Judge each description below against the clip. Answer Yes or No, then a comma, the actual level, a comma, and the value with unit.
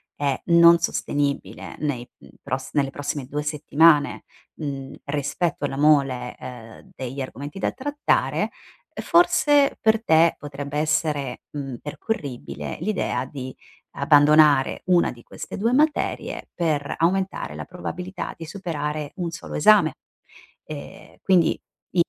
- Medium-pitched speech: Yes, medium, 150 Hz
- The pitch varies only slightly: No, average, 3.7 semitones